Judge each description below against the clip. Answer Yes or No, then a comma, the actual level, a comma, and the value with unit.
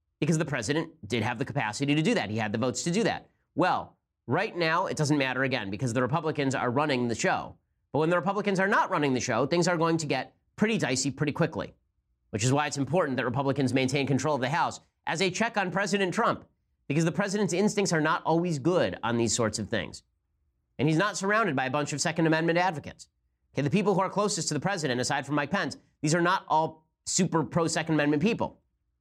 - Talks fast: Yes, fast, 235 wpm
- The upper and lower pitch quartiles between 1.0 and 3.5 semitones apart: No, average, 5.3 semitones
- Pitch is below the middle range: No, medium, 150 Hz